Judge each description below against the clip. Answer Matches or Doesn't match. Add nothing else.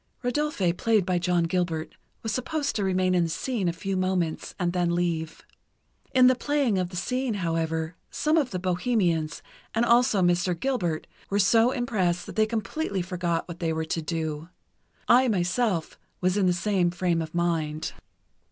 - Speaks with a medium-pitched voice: Matches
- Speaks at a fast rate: Doesn't match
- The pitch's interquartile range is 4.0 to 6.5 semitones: Matches